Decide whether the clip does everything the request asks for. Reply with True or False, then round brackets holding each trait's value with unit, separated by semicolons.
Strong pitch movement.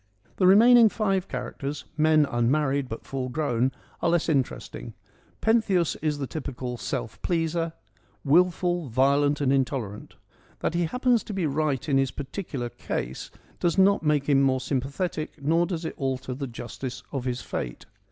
False (4.6 semitones)